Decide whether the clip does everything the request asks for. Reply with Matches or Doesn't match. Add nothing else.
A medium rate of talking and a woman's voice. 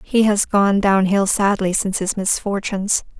Matches